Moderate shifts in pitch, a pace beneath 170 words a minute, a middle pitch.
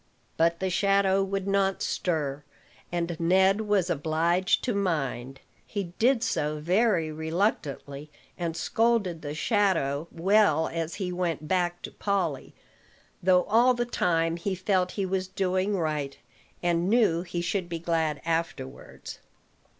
Yes: average, 3.3 semitones; slow, 135 wpm; medium, 175 Hz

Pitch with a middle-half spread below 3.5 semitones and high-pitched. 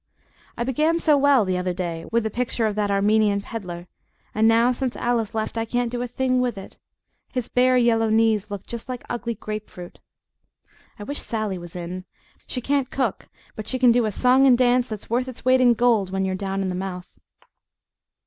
No: average, 3.8 semitones; high, 225 Hz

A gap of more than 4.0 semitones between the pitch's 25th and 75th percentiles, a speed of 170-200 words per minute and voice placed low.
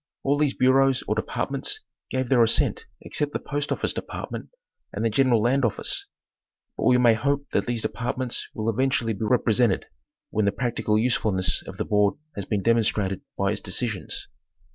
No: average, 3.5 semitones; average, 175 wpm; low, 115 Hz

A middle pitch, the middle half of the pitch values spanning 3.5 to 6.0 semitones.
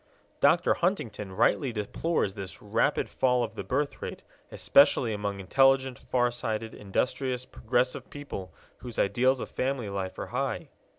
No: low, 125 Hz; average, 4.4 semitones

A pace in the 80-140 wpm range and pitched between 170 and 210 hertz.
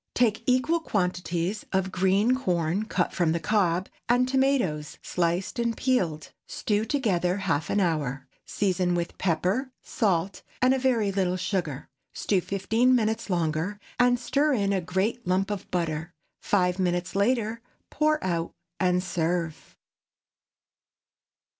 Yes: slow, 135 wpm; high, 190 Hz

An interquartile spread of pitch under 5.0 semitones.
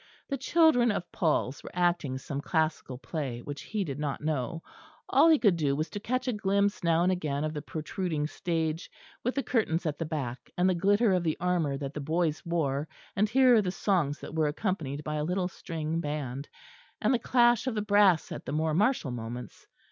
No: average, 5.3 semitones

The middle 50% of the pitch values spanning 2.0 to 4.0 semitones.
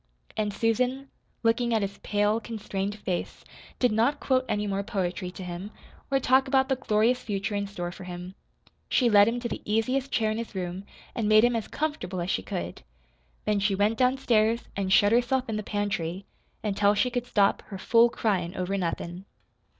Yes: average, 3.6 semitones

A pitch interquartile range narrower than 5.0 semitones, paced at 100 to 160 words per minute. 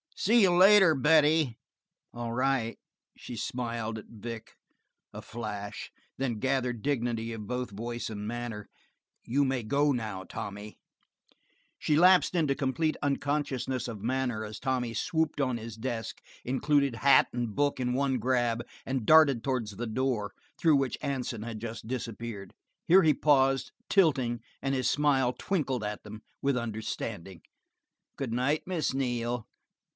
Yes: average, 3.5 semitones; average, 145 wpm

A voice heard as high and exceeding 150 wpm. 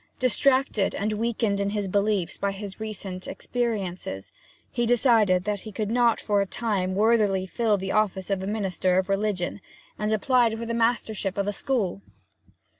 Yes: high, 210 Hz; average, 170 wpm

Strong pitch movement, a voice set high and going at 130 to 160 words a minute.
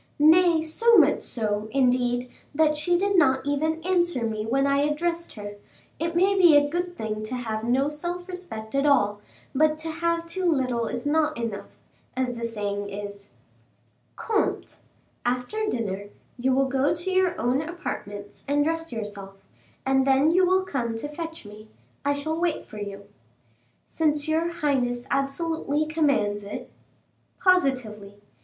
Yes: wide, 6.1 semitones; very high, 285 Hz; average, 155 wpm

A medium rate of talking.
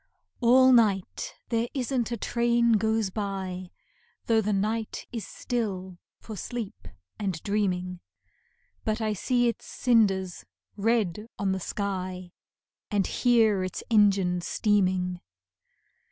No: slow, 115 wpm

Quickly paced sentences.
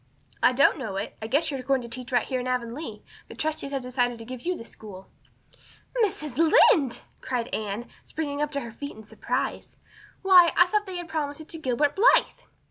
Yes: fast, 210 wpm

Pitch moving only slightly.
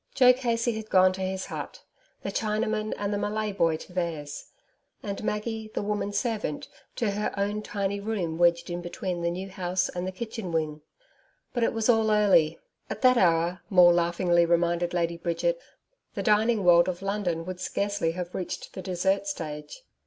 No: average, 3.6 semitones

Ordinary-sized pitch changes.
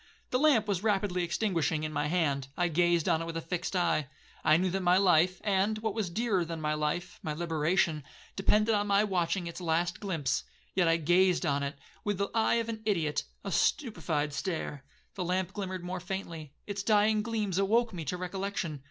Yes: average, 3.7 semitones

